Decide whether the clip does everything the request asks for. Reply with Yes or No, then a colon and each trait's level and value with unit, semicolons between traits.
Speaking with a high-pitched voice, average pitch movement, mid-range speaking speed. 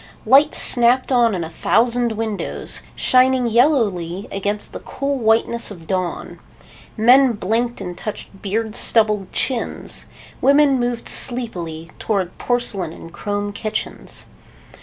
No: high, 225 Hz; average, 3.8 semitones; slow, 120 wpm